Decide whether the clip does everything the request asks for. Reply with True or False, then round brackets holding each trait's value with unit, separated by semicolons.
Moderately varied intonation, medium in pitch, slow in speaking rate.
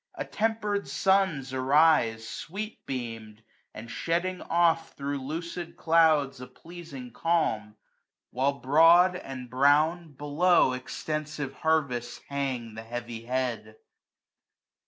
True (5.0 semitones; 145 Hz; 105 wpm)